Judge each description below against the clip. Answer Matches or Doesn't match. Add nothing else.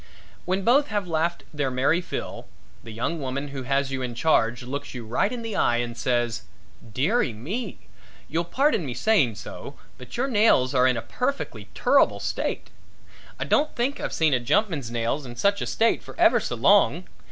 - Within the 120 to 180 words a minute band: Doesn't match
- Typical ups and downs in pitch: Doesn't match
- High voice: Doesn't match